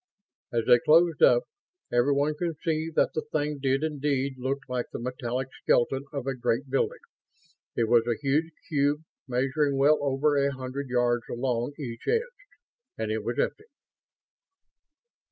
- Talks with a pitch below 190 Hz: Yes, low, 135 Hz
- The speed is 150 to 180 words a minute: Yes, average, 155 wpm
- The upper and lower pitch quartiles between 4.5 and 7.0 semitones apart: No, average, 3.2 semitones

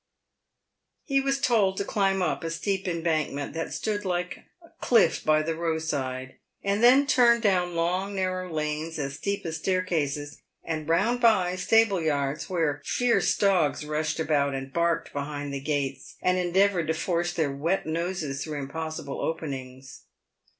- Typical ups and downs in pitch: Yes, average, 4.3 semitones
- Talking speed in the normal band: Yes, average, 155 wpm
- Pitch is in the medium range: Yes, medium, 165 Hz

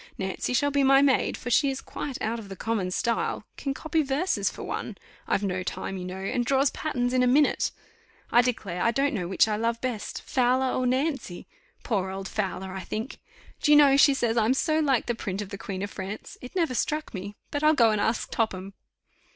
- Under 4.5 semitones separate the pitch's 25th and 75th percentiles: No, wide, 5.5 semitones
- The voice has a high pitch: Yes, high, 240 Hz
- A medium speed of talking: No, fast, 225 wpm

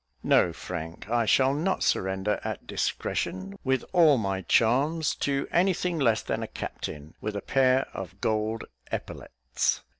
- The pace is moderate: Yes, average, 150 wpm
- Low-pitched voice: Yes, low, 110 Hz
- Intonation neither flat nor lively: No, wide, 6.4 semitones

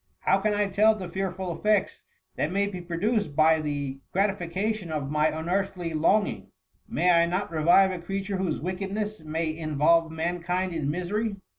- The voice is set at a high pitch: No, medium, 180 Hz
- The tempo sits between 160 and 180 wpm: Yes, average, 165 wpm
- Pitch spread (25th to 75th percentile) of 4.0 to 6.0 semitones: No, average, 3.5 semitones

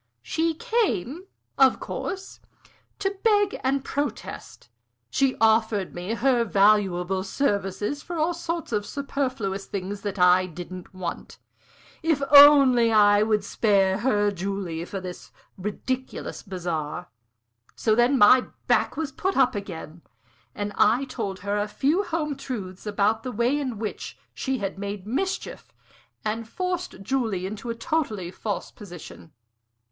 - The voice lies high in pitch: Yes, high, 215 Hz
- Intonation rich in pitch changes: Yes, wide, 5.9 semitones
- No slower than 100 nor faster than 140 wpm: Yes, slow, 135 wpm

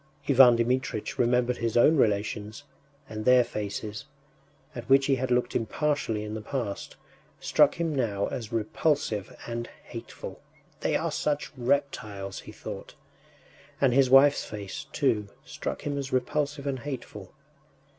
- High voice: No, low, 125 Hz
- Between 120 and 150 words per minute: Yes, average, 140 wpm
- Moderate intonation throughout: Yes, average, 4.2 semitones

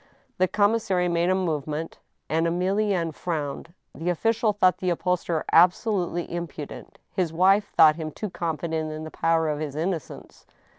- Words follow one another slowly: No, average, 150 wpm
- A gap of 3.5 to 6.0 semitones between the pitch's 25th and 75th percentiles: No, average, 2.7 semitones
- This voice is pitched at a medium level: Yes, medium, 170 Hz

